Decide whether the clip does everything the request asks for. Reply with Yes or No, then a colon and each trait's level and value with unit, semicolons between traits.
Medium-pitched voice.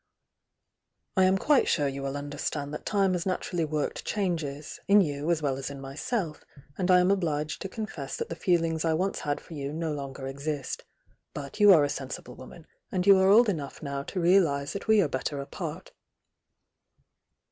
Yes: medium, 155 Hz